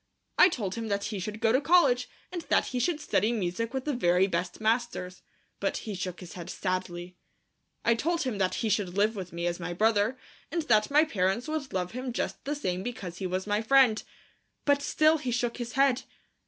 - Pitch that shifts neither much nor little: No, wide, 5.9 semitones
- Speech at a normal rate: No, fast, 215 wpm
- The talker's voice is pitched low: No, high, 220 Hz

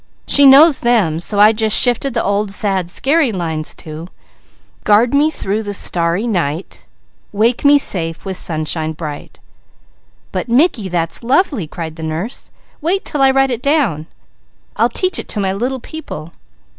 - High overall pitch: Yes, high, 210 Hz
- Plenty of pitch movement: Yes, wide, 8.0 semitones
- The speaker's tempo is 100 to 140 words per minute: No, average, 160 wpm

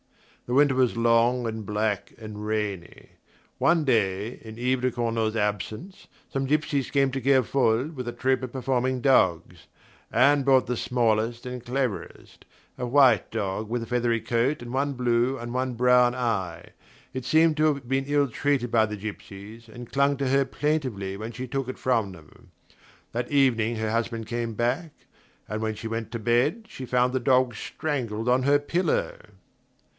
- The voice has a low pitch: Yes, low, 120 Hz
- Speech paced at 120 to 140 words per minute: No, average, 175 wpm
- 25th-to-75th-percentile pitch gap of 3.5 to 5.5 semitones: No, average, 3.1 semitones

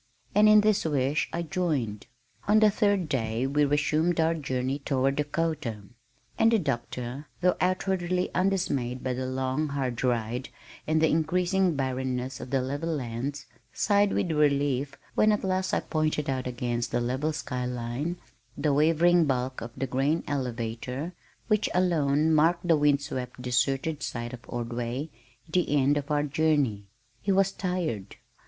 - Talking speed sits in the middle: Yes, average, 155 wpm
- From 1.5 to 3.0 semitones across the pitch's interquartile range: No, average, 4.7 semitones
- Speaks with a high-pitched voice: No, medium, 145 Hz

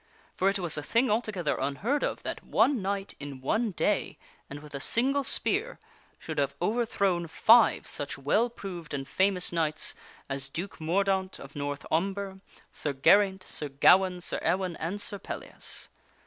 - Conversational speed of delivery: Yes, average, 160 wpm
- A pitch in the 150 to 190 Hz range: Yes, medium, 185 Hz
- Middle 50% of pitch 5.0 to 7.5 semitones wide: Yes, average, 5.3 semitones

